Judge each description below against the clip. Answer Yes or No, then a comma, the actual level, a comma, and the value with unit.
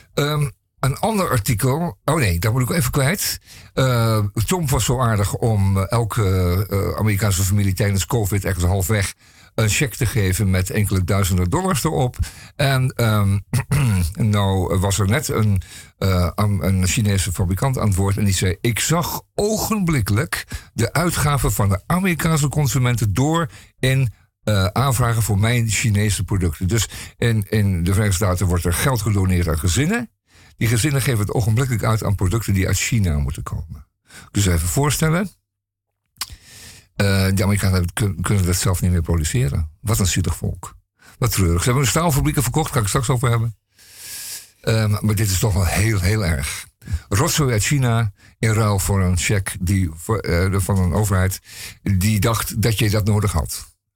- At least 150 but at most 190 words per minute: Yes, average, 170 wpm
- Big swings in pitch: No, average, 4.0 semitones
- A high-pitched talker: No, low, 105 Hz